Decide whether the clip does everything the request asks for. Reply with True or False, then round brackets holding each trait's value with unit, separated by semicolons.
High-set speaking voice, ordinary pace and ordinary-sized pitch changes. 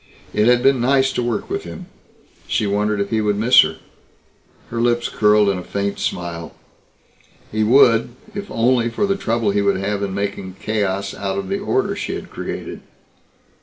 False (105 Hz; 185 wpm; 3.2 semitones)